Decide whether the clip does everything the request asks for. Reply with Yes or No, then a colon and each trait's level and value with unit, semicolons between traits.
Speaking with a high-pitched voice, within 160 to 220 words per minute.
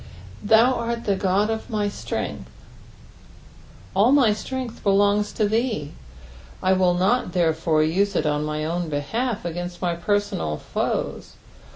No: high, 195 Hz; average, 140 wpm